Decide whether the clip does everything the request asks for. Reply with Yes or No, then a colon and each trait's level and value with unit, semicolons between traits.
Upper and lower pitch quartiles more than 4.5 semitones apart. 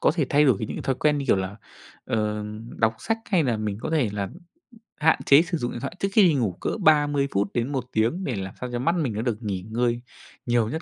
Yes: wide, 5.6 semitones